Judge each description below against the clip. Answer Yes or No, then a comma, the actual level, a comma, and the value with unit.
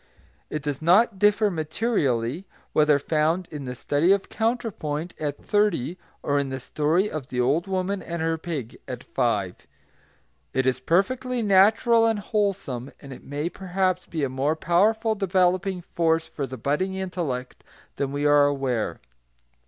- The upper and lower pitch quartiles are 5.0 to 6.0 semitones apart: Yes, average, 5.3 semitones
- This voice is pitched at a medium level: Yes, medium, 165 Hz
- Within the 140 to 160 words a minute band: Yes, average, 155 wpm